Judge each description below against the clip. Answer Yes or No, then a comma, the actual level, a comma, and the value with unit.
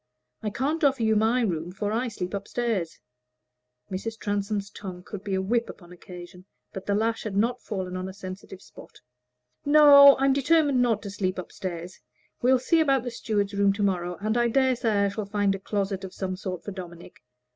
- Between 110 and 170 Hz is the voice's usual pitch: No, high, 205 Hz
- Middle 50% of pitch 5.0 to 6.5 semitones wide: No, average, 4.1 semitones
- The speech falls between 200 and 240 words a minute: Yes, fast, 205 wpm